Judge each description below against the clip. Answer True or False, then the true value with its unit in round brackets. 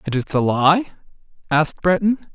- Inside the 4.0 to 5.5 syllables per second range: True (5.2 syllables/s)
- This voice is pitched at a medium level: True (165 Hz)